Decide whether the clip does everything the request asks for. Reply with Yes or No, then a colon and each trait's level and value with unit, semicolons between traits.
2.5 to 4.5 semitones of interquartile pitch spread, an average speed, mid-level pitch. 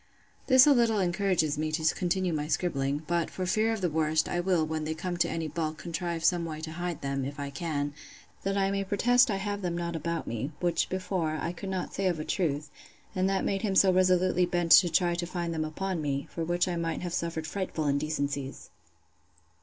No: average, 3.2 semitones; fast, 225 wpm; medium, 170 Hz